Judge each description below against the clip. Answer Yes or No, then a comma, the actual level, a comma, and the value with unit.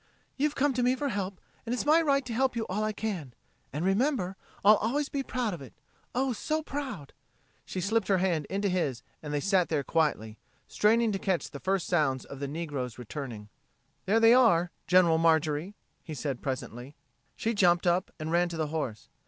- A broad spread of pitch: Yes, wide, 7.1 semitones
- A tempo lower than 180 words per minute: No, average, 200 wpm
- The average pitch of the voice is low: No, medium, 185 Hz